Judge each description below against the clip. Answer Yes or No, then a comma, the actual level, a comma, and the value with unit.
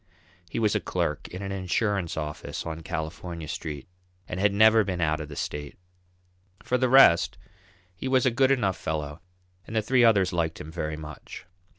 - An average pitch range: No, wide, 5.9 semitones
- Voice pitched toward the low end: Yes, very low, 90 Hz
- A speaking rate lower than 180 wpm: No, average, 185 wpm